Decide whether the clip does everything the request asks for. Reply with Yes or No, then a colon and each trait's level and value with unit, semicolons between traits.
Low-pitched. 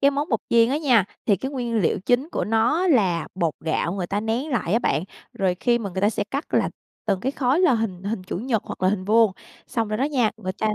No: high, 225 Hz